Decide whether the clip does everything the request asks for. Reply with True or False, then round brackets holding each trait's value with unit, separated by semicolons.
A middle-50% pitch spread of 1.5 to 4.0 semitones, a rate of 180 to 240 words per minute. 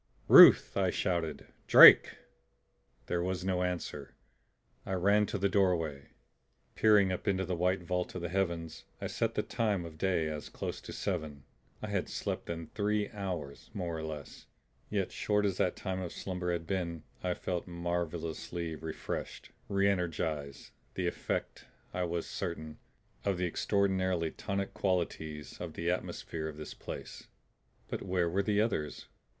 False (2.6 semitones; 155 wpm)